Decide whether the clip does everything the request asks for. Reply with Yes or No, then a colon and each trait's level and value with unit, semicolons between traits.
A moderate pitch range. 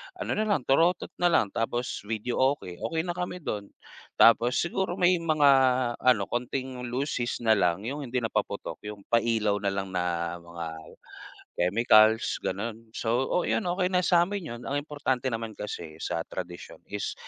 No: wide, 6.5 semitones